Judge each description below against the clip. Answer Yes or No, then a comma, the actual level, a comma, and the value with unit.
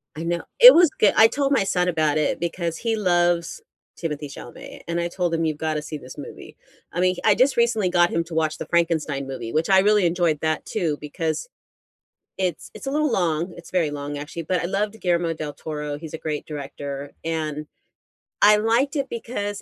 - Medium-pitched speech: Yes, medium, 170 Hz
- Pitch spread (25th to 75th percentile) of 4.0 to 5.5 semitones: Yes, average, 4.9 semitones